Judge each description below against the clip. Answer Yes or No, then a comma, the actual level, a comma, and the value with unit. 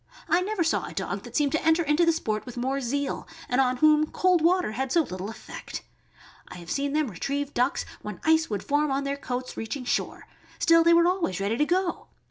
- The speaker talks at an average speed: No, fast, 230 wpm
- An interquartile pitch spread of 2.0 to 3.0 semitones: No, average, 4.8 semitones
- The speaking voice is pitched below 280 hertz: No, very high, 285 Hz